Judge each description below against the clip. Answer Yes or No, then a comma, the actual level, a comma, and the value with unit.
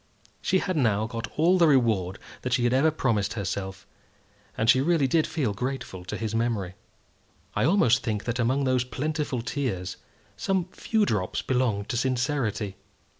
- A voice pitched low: Yes, low, 125 Hz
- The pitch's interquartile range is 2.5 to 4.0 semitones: No, average, 4.8 semitones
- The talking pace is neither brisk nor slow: Yes, average, 165 wpm